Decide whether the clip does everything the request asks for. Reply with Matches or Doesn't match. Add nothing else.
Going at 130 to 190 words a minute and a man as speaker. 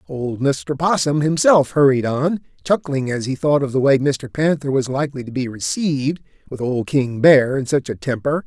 Doesn't match